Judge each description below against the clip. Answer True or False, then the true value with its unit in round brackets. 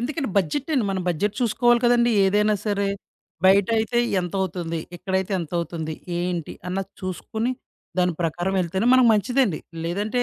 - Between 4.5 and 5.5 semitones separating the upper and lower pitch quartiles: True (4.8 semitones)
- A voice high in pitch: True (195 Hz)